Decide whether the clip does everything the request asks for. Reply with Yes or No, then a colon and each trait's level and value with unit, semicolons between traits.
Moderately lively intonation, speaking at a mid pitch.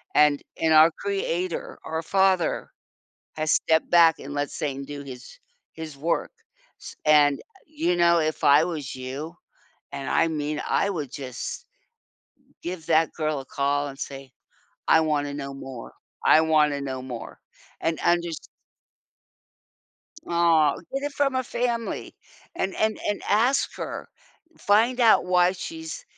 Yes: average, 4.3 semitones; medium, 160 Hz